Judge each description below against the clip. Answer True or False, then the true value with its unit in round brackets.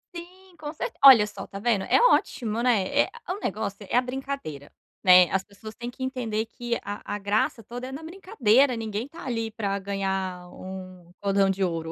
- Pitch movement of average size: True (4.8 semitones)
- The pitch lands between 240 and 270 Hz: False (220 Hz)